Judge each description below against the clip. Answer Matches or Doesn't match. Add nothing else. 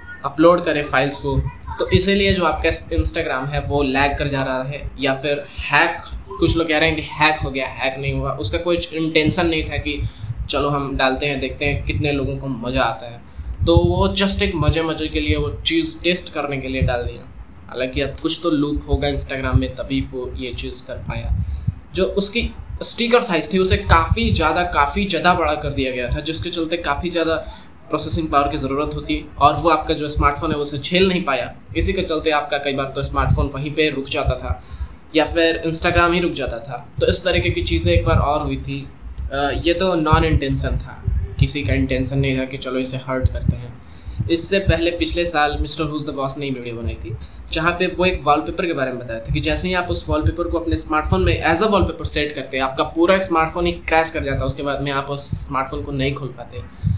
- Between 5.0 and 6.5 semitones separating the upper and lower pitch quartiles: Doesn't match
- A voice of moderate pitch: Matches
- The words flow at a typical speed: Doesn't match